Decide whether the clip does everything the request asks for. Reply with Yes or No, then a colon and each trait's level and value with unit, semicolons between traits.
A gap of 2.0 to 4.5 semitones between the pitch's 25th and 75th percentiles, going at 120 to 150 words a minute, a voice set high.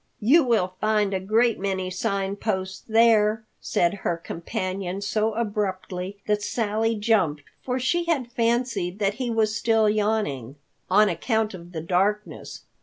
Yes: average, 3.1 semitones; average, 145 wpm; high, 210 Hz